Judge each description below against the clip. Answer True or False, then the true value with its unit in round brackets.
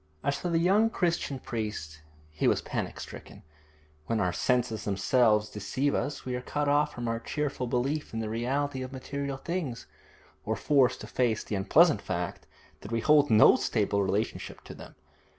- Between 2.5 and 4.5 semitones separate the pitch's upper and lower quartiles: False (5.0 semitones)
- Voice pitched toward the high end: False (125 Hz)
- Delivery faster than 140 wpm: True (175 wpm)